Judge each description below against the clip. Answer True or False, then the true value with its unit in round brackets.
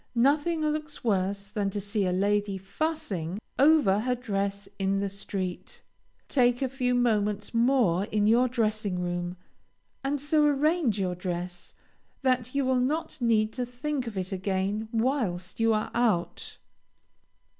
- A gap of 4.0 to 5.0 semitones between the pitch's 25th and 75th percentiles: True (4.7 semitones)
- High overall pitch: True (220 Hz)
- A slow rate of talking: False (145 wpm)